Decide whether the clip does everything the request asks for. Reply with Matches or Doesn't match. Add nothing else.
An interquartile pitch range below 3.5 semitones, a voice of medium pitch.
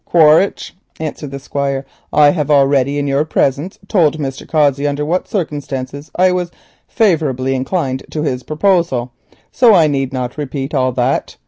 Matches